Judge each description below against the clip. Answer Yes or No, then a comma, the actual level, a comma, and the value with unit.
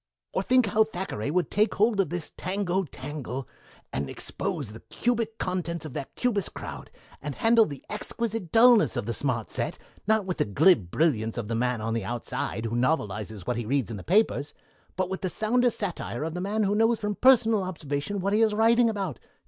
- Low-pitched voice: No, medium, 180 Hz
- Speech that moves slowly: No, fast, 205 wpm